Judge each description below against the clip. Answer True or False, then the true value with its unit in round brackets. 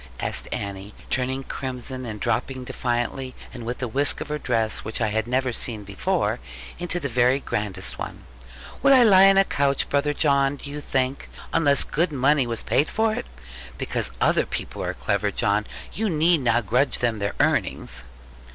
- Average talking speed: True (180 wpm)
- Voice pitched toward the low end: True (130 Hz)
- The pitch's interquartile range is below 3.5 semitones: False (4.2 semitones)